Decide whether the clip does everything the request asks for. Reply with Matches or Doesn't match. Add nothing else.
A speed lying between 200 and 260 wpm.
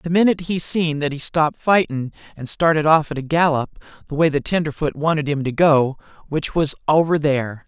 Matches